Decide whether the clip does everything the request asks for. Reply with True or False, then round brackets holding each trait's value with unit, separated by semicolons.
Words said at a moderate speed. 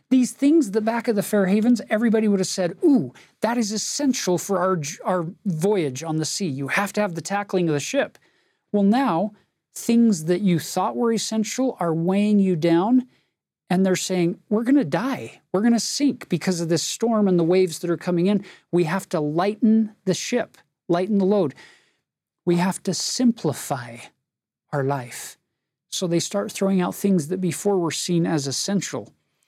True (190 wpm)